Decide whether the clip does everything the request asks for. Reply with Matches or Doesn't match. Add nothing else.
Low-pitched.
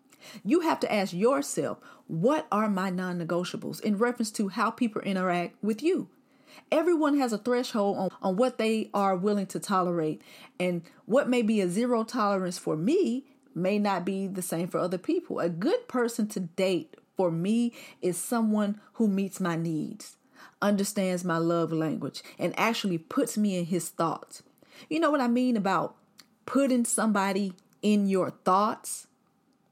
Doesn't match